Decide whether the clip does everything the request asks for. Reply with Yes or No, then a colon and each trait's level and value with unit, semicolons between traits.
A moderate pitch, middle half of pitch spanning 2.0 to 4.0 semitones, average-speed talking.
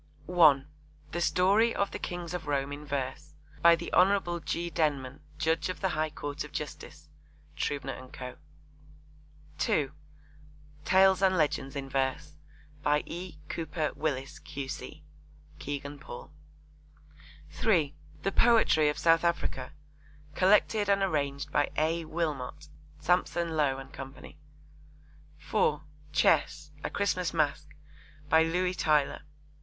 No: medium, 155 Hz; average, 3.7 semitones; slow, 125 wpm